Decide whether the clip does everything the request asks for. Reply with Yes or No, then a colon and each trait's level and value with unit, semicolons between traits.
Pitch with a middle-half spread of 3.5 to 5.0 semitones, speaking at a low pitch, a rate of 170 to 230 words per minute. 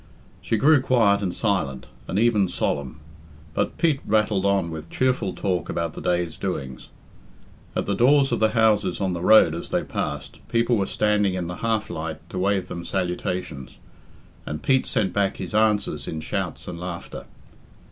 Yes: average, 4.3 semitones; very low, 95 Hz; average, 175 wpm